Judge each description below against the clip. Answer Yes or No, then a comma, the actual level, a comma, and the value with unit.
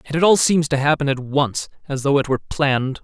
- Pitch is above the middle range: No, medium, 140 Hz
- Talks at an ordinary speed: No, fast, 255 wpm